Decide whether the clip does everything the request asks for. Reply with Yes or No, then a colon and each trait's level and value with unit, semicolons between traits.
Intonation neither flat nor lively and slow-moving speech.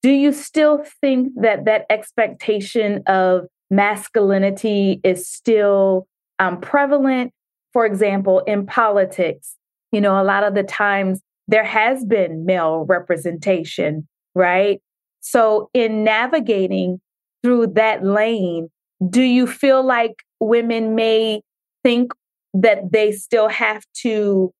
Yes: average, 3.2 semitones; slow, 115 wpm